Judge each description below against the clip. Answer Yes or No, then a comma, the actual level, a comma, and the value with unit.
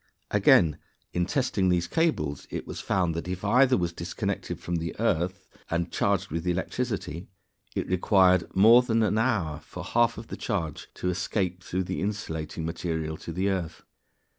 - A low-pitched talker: Yes, very low, 90 Hz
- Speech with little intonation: No, average, 3.9 semitones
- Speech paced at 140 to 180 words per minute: Yes, average, 165 wpm